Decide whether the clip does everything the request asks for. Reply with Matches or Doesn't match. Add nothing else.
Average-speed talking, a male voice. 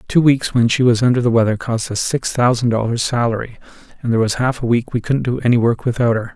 Doesn't match